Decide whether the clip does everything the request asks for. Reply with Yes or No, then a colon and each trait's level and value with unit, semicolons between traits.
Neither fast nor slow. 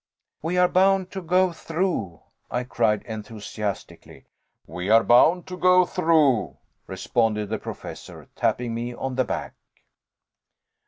No: slow, 125 wpm